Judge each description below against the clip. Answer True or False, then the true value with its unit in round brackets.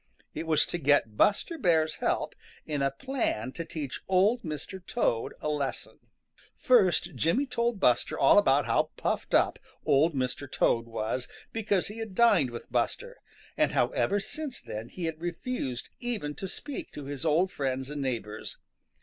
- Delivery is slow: False (165 wpm)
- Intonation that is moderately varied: False (7.1 semitones)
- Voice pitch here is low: False (160 Hz)